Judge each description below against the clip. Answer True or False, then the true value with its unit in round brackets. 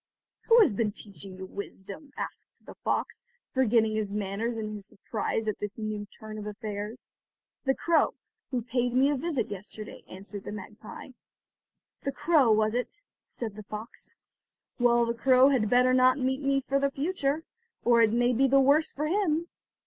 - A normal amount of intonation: True (4.4 semitones)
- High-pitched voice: True (235 Hz)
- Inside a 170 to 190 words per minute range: True (175 wpm)